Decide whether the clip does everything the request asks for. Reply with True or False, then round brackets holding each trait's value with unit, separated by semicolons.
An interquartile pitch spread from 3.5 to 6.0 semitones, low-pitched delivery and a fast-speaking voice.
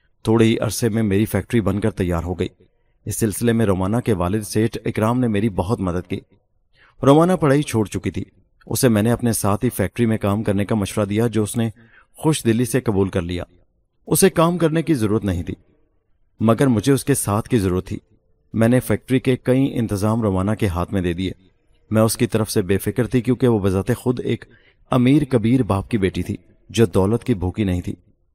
True (3.8 semitones; 110 Hz; 220 wpm)